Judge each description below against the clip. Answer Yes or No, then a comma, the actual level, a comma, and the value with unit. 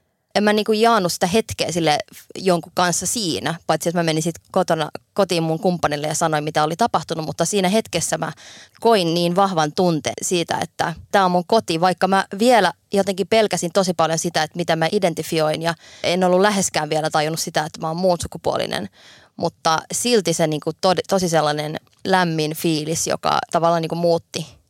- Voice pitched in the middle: Yes, medium, 170 Hz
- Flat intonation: No, average, 3.0 semitones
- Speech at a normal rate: No, fast, 180 wpm